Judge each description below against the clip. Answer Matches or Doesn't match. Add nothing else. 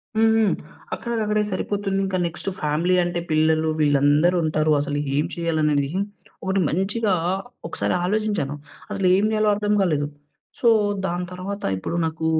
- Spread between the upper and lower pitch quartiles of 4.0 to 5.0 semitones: Matches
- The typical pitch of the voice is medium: Matches